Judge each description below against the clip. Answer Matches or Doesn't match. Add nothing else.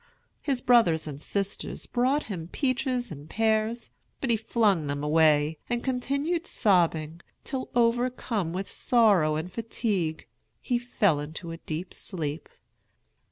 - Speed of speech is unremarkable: Doesn't match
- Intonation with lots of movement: Matches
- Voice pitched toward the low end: Doesn't match